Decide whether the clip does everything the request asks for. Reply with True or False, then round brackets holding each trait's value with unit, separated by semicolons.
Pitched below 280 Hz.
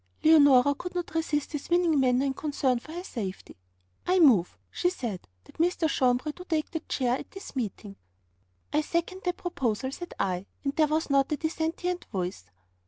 False (295 Hz)